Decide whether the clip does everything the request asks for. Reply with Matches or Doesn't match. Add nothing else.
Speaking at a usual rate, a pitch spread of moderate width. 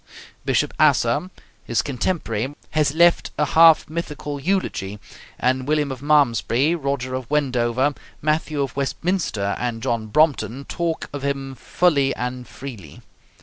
Doesn't match